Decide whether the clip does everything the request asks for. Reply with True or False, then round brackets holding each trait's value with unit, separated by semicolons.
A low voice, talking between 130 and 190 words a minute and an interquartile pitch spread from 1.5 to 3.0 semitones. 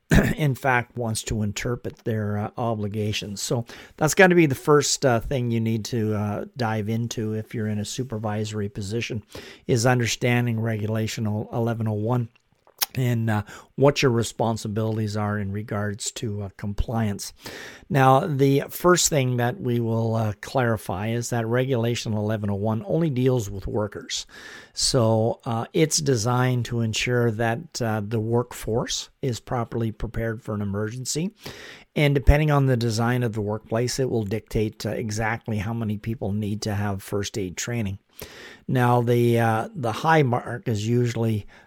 True (115 Hz; 155 wpm; 2.6 semitones)